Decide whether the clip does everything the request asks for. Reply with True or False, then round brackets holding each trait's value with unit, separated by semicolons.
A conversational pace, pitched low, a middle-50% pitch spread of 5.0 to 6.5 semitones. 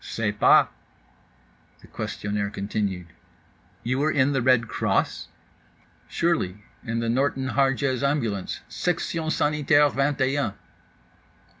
False (110 wpm; 130 Hz; 5.3 semitones)